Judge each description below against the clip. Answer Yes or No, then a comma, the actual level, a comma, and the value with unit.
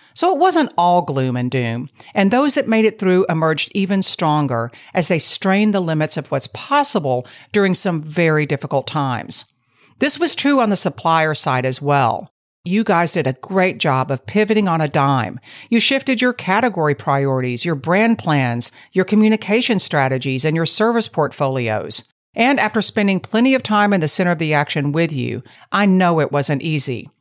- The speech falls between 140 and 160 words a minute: No, average, 185 wpm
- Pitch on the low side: No, medium, 165 Hz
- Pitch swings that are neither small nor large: No, wide, 7.1 semitones